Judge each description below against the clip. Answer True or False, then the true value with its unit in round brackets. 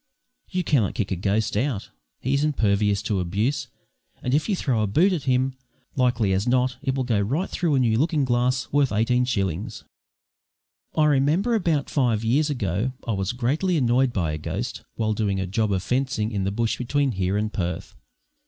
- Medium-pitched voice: False (120 Hz)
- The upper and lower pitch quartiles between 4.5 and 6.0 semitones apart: True (5.1 semitones)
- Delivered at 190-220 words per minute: True (195 wpm)